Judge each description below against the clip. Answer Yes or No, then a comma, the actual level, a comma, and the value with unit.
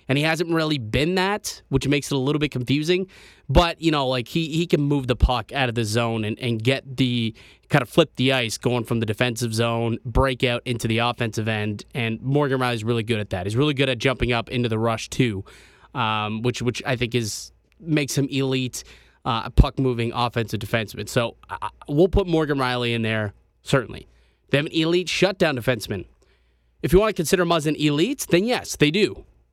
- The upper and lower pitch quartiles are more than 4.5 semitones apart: No, average, 4.1 semitones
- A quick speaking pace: Yes, fast, 210 wpm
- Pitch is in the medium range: No, low, 125 Hz